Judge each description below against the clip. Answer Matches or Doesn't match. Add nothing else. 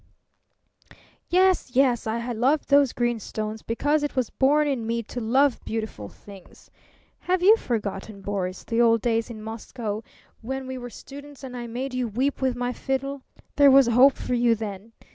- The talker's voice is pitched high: Matches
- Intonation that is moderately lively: Matches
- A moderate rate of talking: Matches